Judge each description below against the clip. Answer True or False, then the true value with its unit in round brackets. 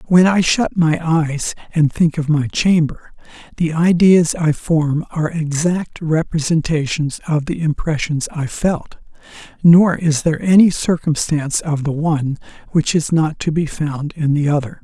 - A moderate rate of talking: True (160 wpm)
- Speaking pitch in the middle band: True (160 Hz)